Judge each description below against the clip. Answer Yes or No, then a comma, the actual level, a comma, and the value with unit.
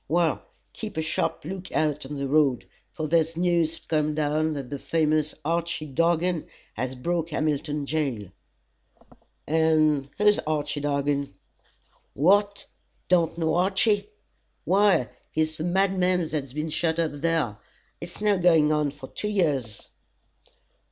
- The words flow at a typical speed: No, slow, 130 wpm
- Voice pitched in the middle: Yes, medium, 155 Hz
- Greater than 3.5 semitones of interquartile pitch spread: No, average, 2.8 semitones